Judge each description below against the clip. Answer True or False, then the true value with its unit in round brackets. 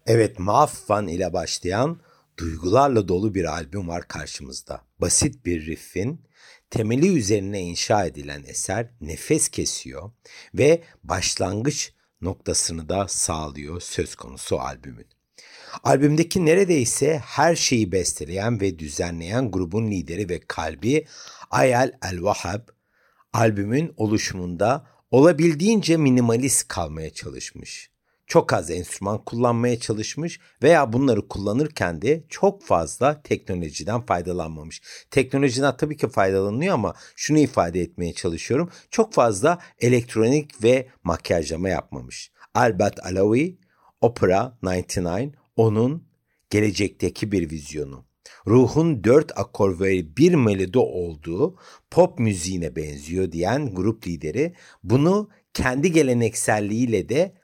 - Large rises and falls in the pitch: True (7.7 semitones)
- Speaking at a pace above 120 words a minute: False (105 wpm)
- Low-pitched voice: True (110 Hz)